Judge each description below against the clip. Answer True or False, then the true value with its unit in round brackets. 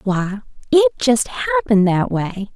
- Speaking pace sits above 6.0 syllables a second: False (4.1 syllables/s)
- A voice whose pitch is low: False (200 Hz)